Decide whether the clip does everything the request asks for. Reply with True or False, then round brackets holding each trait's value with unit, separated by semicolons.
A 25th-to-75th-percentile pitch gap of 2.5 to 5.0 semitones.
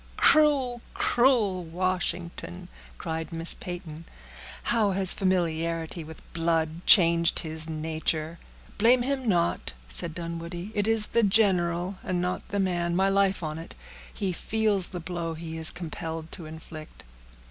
True (3.2 semitones)